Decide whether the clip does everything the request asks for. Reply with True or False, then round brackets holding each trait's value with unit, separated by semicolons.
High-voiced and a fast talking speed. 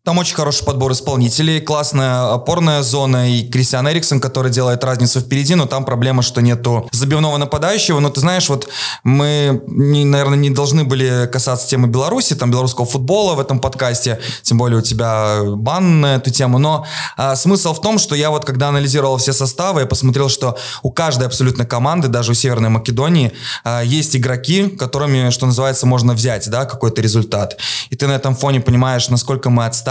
False (135 Hz; 185 wpm)